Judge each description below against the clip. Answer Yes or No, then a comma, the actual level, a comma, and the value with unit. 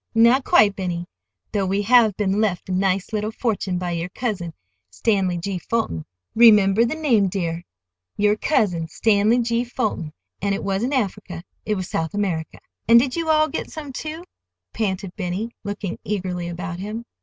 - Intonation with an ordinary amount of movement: Yes, average, 4.2 semitones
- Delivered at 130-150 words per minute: No, average, 165 wpm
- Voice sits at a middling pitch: No, high, 200 Hz